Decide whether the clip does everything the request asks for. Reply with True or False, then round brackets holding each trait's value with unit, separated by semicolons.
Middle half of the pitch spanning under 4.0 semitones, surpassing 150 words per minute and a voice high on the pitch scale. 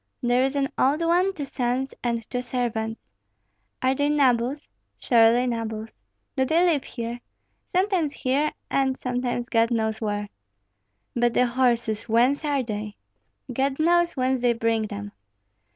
False (3.3 semitones; 145 wpm; 250 Hz)